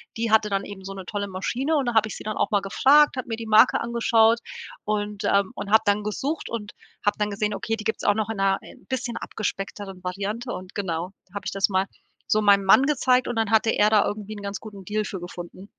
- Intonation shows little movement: Yes, narrow, 2.2 semitones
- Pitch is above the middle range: Yes, high, 210 Hz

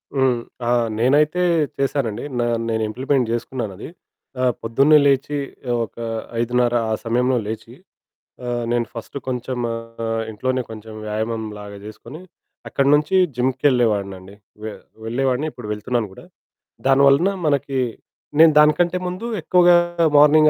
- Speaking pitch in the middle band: No, low, 125 Hz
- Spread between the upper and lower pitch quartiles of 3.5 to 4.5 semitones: Yes, average, 3.8 semitones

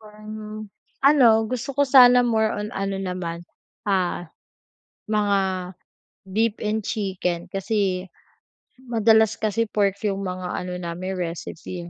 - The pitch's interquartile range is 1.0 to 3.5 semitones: Yes, average, 3.1 semitones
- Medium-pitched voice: No, high, 205 Hz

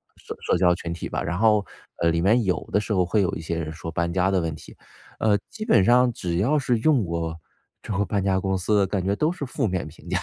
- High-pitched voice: No, very low, 95 Hz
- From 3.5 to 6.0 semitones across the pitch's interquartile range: Yes, average, 4.3 semitones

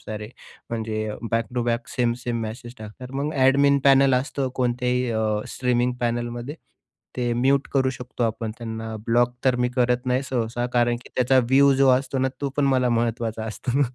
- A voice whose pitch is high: No, low, 125 Hz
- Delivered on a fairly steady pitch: Yes, narrow, 2.0 semitones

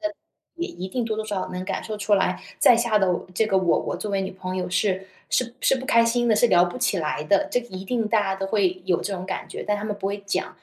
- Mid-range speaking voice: No, high, 200 Hz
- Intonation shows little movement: No, average, 3.3 semitones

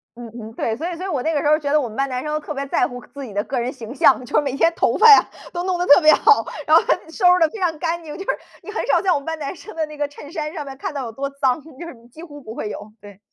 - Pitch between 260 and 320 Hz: Yes, very high, 295 Hz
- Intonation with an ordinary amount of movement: Yes, average, 4.3 semitones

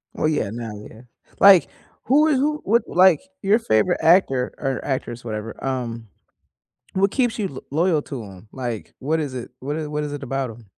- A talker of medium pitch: Yes, medium, 145 Hz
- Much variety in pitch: Yes, wide, 7.8 semitones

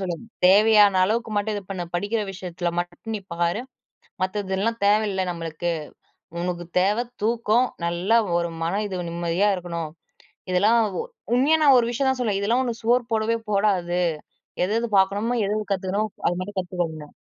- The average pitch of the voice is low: No, high, 200 Hz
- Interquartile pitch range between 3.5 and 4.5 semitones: Yes, average, 4.0 semitones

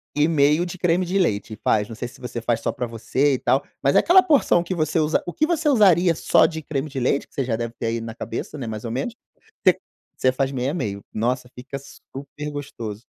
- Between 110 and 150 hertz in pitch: Yes, medium, 140 Hz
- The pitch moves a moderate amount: No, wide, 5.9 semitones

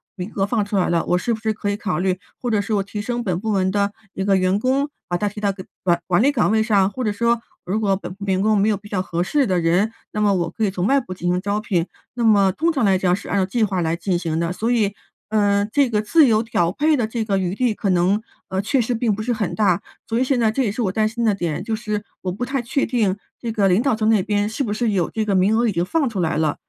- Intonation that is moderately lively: Yes, average, 3.2 semitones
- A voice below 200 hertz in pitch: No, high, 205 Hz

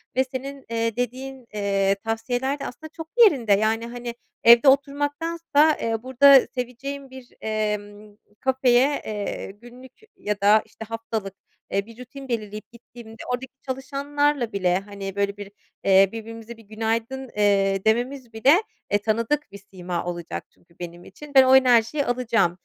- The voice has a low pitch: No, high, 230 Hz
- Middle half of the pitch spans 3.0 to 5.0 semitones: Yes, average, 4.2 semitones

